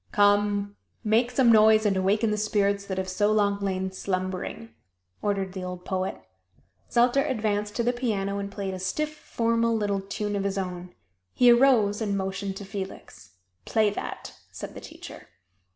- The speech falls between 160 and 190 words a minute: Yes, average, 170 wpm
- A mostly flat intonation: Yes, narrow, 2.2 semitones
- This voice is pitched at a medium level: No, high, 205 Hz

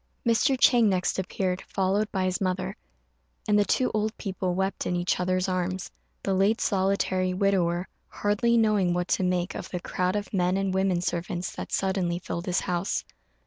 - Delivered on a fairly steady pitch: Yes, narrow, 1.7 semitones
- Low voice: No, high, 190 Hz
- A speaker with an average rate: Yes, average, 180 wpm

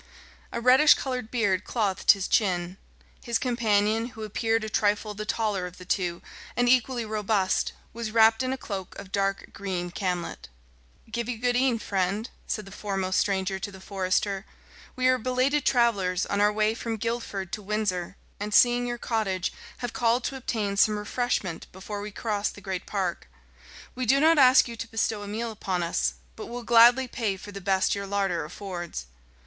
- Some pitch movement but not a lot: Yes, average, 3.5 semitones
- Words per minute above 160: Yes, average, 185 wpm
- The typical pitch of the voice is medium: No, high, 210 Hz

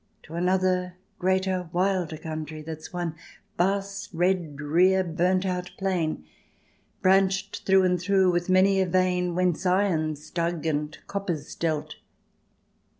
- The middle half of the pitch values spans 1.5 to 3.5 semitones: Yes, narrow, 2.5 semitones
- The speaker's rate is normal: No, slow, 125 wpm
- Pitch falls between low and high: Yes, medium, 180 Hz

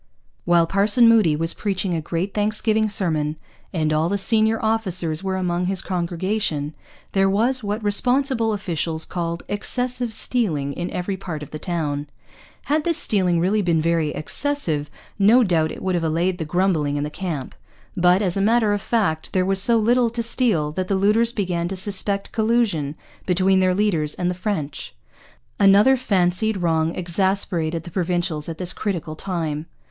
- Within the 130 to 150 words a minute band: No, average, 170 wpm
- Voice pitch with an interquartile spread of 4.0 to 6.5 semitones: Yes, average, 4.3 semitones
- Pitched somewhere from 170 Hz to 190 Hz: Yes, medium, 185 Hz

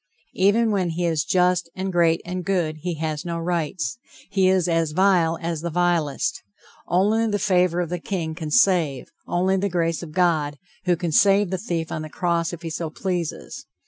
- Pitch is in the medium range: Yes, medium, 175 Hz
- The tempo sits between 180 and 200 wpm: Yes, average, 195 wpm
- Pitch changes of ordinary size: No, narrow, 2.3 semitones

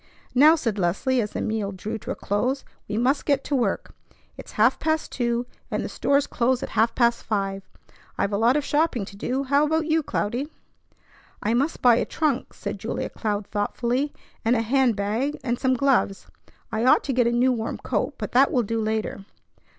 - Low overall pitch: No, high, 240 Hz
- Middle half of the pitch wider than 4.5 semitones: No, average, 4.0 semitones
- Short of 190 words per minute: No, fast, 205 wpm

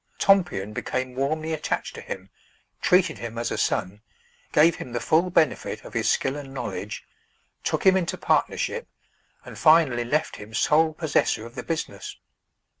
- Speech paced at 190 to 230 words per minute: No, average, 160 wpm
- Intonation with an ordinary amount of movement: No, wide, 5.7 semitones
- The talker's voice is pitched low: No, medium, 145 Hz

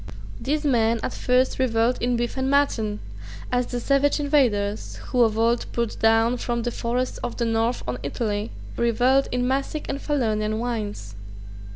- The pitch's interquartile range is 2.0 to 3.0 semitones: Yes, narrow, 2.5 semitones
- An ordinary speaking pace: Yes, average, 165 wpm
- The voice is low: No, high, 240 Hz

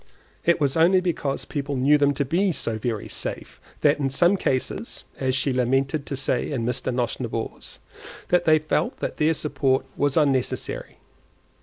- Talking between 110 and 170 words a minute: Yes, average, 160 wpm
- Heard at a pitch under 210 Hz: Yes, medium, 140 Hz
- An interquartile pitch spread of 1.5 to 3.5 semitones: Yes, average, 3.2 semitones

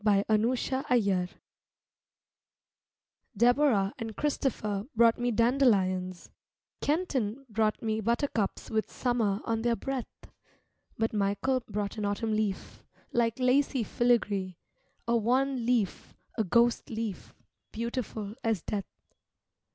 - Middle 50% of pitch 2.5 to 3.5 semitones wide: Yes, average, 3.1 semitones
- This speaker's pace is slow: Yes, slow, 105 wpm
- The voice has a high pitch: Yes, high, 225 Hz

